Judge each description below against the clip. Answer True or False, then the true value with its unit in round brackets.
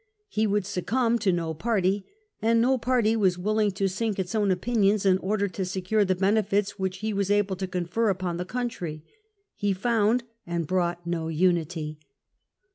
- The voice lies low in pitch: False (195 Hz)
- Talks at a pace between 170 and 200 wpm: True (175 wpm)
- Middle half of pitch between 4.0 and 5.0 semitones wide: False (3.2 semitones)